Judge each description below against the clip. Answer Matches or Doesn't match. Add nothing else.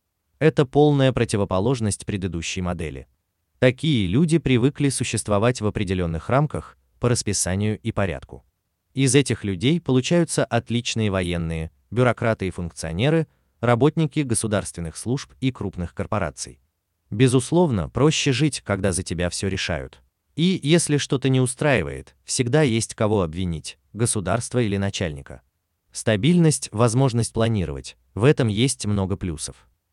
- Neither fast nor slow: Matches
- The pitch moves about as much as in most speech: Doesn't match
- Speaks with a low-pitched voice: Matches